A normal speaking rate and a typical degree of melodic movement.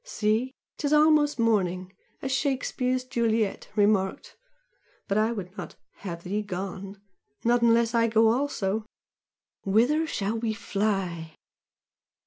No: slow, 115 wpm; average, 4.2 semitones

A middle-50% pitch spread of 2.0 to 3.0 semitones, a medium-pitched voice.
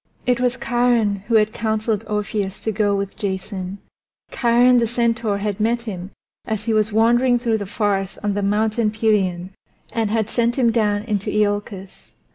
No: narrow, 2.4 semitones; high, 215 Hz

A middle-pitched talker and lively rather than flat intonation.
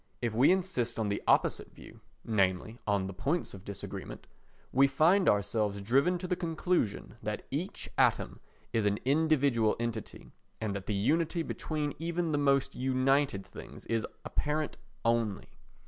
No: low, 130 Hz; wide, 6.6 semitones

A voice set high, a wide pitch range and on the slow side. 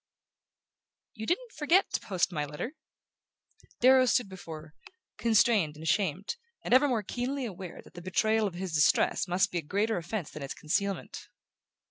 No: high, 195 Hz; wide, 5.8 semitones; average, 165 wpm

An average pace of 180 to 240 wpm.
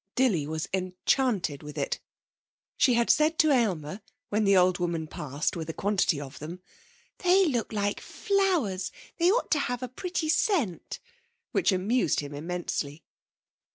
No: average, 155 wpm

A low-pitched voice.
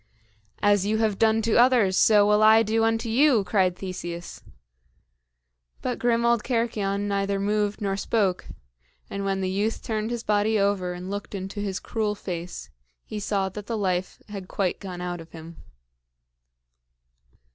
No: high, 205 Hz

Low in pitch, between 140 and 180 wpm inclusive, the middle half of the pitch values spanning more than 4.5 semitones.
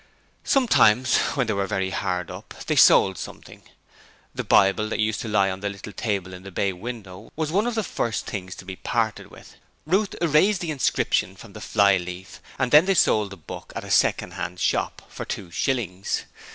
No: low, 105 Hz; fast, 205 wpm; average, 5.2 semitones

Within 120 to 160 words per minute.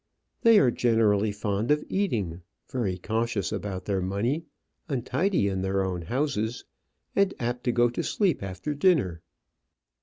Yes: average, 145 wpm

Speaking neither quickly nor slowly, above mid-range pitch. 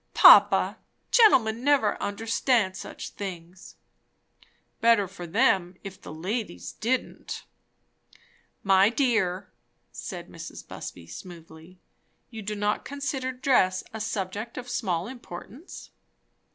No: slow, 105 wpm; high, 205 Hz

